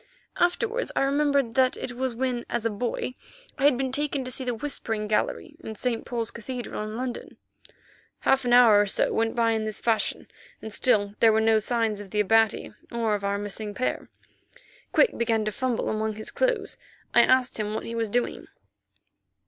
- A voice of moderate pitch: No, high, 230 Hz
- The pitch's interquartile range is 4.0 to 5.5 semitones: No, average, 3.0 semitones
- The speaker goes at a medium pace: Yes, average, 195 wpm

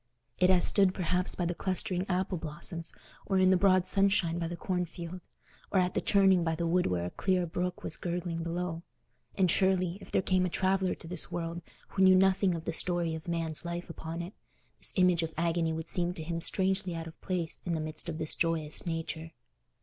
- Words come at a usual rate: No, fast, 215 wpm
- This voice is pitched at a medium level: Yes, medium, 175 Hz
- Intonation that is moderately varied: No, narrow, 2.0 semitones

